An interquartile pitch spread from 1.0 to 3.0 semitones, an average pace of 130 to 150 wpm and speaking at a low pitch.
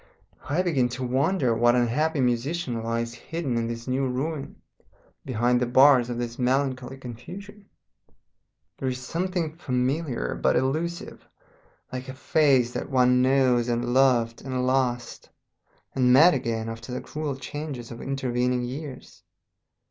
Yes: narrow, 2.6 semitones; average, 140 wpm; low, 130 Hz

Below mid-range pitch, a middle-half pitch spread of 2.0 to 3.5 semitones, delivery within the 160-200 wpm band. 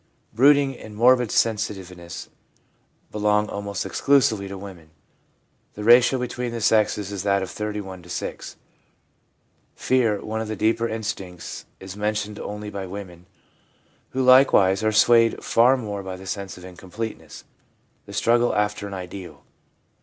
No: low, 105 Hz; average, 2.9 semitones; average, 145 wpm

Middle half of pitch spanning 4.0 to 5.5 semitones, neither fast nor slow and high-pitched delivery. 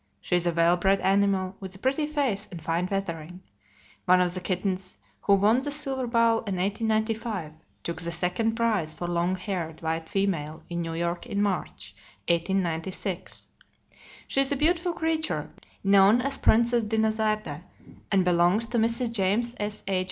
Yes: average, 4.5 semitones; average, 160 wpm; high, 195 Hz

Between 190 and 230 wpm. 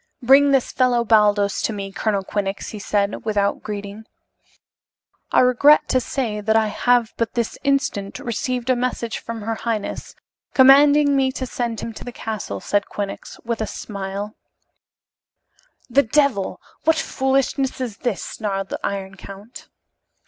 No: average, 150 wpm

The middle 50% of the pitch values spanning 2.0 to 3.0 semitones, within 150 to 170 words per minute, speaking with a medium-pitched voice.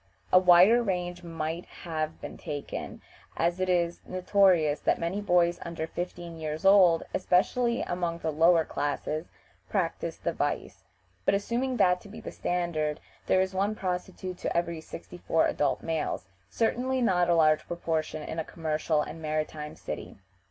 Yes: average, 2.7 semitones; average, 160 wpm; medium, 175 Hz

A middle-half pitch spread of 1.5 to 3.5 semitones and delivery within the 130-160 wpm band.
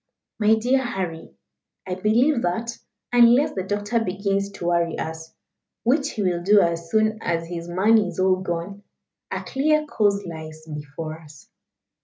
No: average, 4.7 semitones; average, 155 wpm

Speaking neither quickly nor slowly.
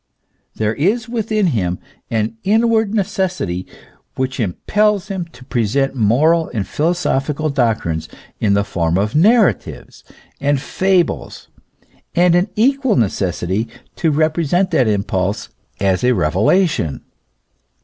No: slow, 120 wpm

